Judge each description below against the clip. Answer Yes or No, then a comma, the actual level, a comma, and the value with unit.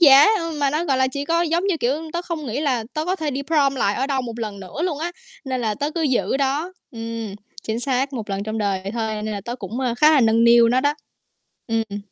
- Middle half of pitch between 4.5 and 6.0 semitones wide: Yes, average, 4.9 semitones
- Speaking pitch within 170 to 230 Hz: No, very high, 260 Hz